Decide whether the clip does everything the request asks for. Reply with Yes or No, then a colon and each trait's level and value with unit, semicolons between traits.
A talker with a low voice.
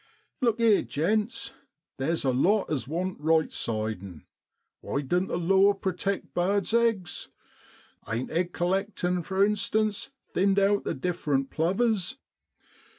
No: medium, 185 Hz